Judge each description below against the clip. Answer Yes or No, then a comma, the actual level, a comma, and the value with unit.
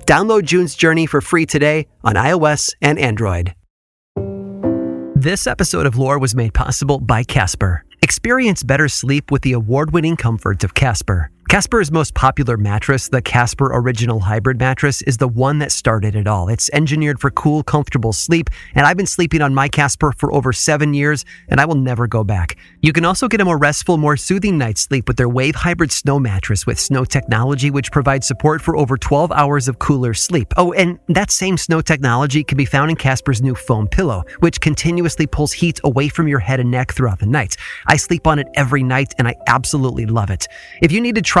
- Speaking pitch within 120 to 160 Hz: Yes, medium, 140 Hz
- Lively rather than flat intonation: No, average, 4.4 semitones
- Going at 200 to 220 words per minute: Yes, fast, 205 wpm